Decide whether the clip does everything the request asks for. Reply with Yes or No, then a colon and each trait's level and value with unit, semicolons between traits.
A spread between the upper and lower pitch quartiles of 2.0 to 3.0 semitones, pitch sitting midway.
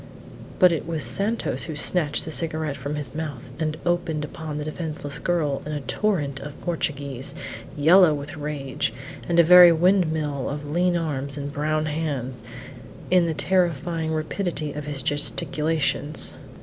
Yes: average, 2.7 semitones; medium, 155 Hz